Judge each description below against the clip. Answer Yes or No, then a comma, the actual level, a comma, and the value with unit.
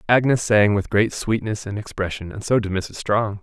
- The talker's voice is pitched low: Yes, low, 105 Hz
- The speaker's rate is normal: No, fast, 210 wpm